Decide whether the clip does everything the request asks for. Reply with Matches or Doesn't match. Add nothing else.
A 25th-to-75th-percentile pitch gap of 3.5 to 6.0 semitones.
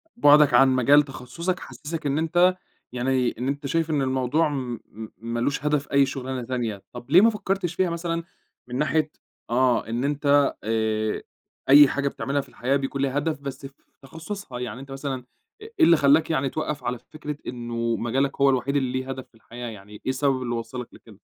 Doesn't match